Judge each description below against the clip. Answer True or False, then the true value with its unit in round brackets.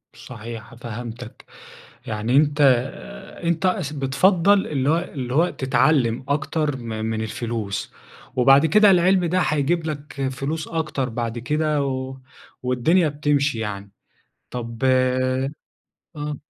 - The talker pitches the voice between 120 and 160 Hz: True (135 Hz)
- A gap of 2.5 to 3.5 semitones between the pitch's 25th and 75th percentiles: False (4.1 semitones)